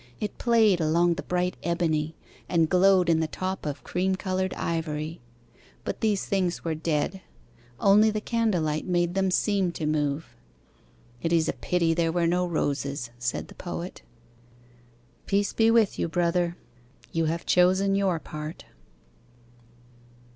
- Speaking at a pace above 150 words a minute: No, average, 145 wpm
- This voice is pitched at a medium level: Yes, medium, 175 Hz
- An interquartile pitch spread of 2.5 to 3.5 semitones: Yes, average, 3.0 semitones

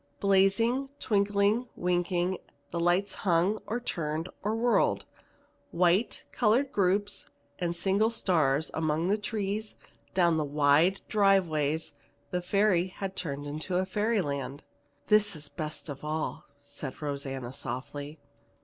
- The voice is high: No, medium, 180 Hz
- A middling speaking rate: No, slow, 125 wpm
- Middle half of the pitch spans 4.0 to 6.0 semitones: Yes, average, 5.0 semitones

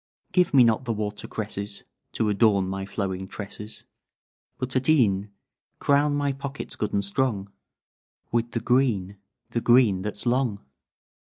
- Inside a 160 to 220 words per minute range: No, average, 145 wpm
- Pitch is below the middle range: Yes, low, 110 Hz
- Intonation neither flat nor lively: Yes, average, 4.4 semitones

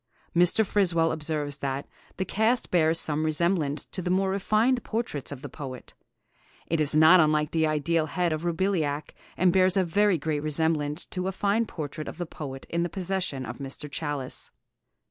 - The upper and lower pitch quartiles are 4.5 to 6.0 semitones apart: No, average, 3.8 semitones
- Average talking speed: Yes, average, 180 wpm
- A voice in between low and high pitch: Yes, medium, 165 Hz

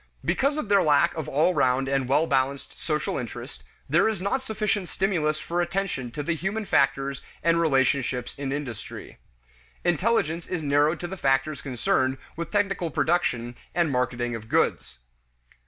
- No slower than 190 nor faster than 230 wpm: No, average, 155 wpm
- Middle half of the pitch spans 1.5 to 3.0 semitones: No, average, 5.0 semitones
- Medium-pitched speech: Yes, medium, 155 Hz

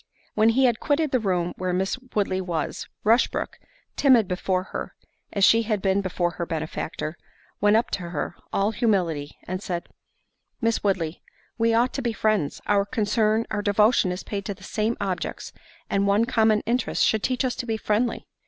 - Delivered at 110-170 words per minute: No, average, 180 wpm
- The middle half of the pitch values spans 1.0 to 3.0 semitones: No, average, 3.6 semitones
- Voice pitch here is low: No, high, 205 Hz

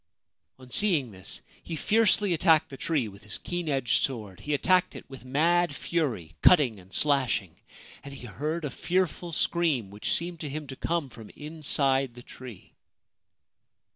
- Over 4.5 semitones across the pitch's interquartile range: Yes, wide, 5.5 semitones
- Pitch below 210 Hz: Yes, medium, 140 Hz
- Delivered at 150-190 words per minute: Yes, average, 165 wpm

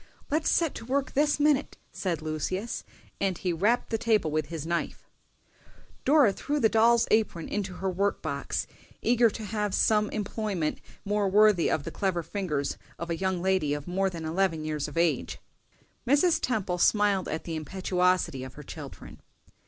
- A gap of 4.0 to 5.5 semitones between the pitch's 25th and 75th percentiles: Yes, average, 4.9 semitones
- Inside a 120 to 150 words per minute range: No, average, 170 wpm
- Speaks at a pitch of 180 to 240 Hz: Yes, high, 190 Hz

